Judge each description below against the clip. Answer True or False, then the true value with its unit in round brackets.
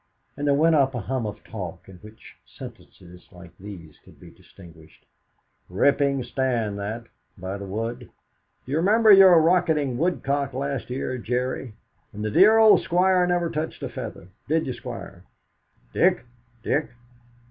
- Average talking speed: True (150 wpm)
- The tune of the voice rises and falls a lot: True (7.4 semitones)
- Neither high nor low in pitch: False (130 Hz)